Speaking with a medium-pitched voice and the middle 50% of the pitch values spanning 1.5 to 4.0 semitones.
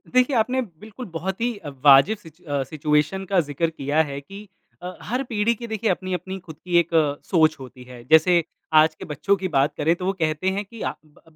No: medium, 170 Hz; average, 4.9 semitones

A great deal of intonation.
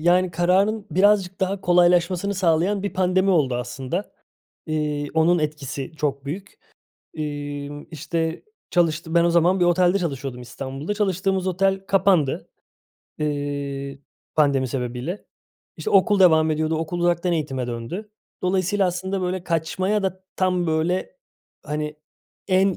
No: average, 4.0 semitones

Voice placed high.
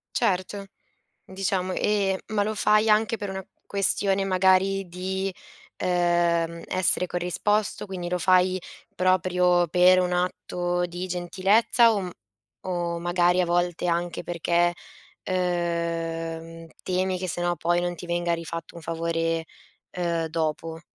No: medium, 180 Hz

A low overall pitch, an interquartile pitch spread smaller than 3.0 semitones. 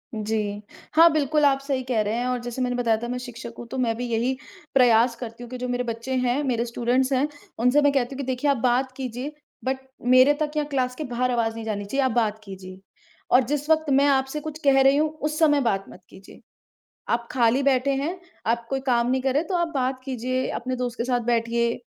No: very high, 250 Hz; narrow, 2.6 semitones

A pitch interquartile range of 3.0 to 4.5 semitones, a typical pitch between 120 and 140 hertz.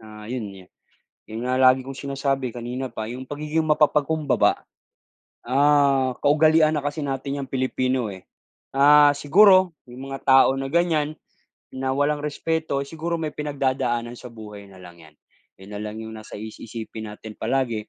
Yes: average, 4.1 semitones; low, 135 Hz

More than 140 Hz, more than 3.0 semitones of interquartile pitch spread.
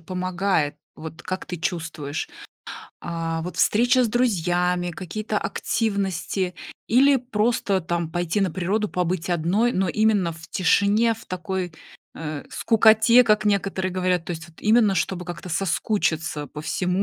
Yes: medium, 185 Hz; average, 3.7 semitones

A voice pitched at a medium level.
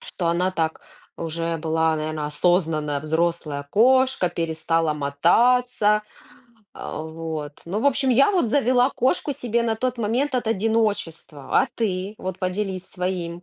Yes: medium, 180 Hz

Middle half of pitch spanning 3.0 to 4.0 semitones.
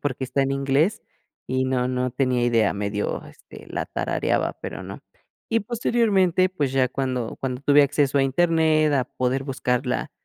Yes: average, 3.4 semitones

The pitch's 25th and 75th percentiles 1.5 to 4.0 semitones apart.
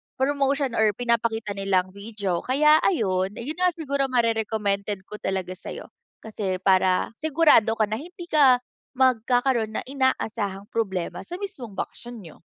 No: average, 5.2 semitones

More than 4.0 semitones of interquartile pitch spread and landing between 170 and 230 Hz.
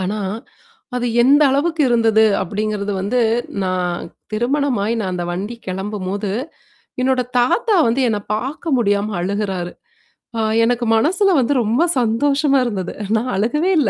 Yes: average, 4.7 semitones; high, 225 Hz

